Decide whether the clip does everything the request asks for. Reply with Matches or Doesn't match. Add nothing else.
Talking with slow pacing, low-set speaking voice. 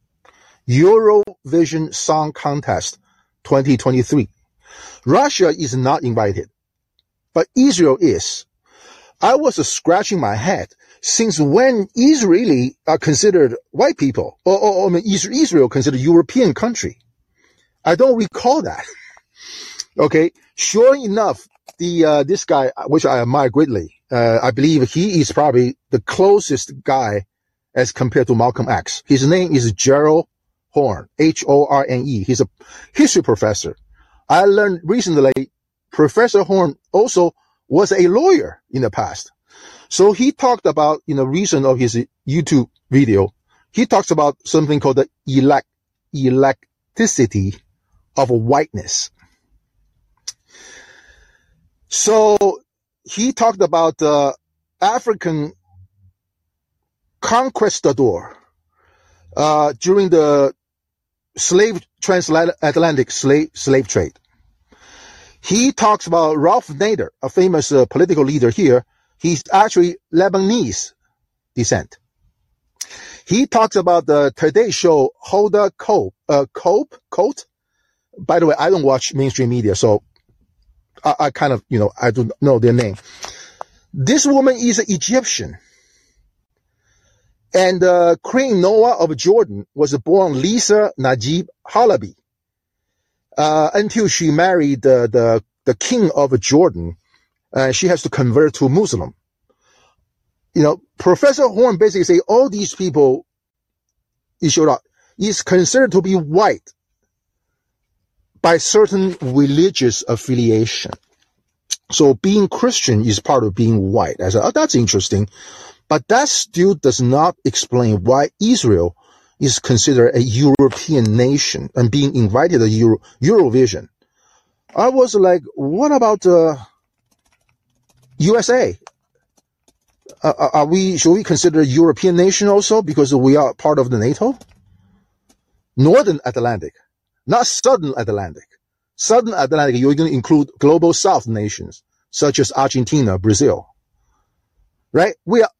Doesn't match